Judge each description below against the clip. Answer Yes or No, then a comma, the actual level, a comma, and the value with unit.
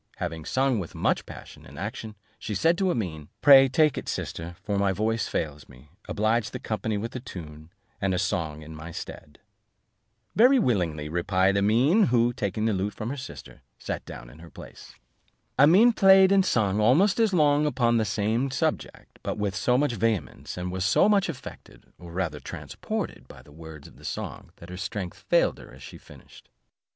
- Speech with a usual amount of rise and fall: No, wide, 7.4 semitones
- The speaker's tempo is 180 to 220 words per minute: Yes, average, 195 wpm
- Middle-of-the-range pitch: No, low, 105 Hz